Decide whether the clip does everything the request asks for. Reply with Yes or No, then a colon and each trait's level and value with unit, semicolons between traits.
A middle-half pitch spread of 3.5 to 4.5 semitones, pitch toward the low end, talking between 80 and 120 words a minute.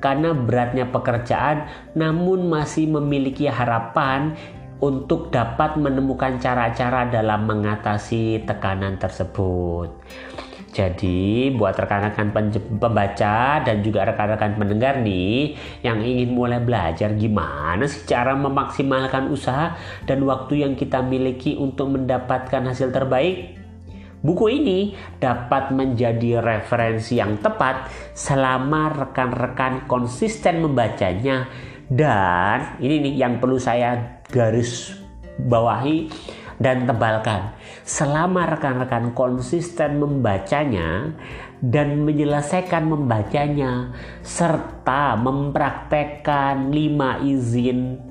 Yes: average, 4.2 semitones; low, 130 Hz; average, 90 wpm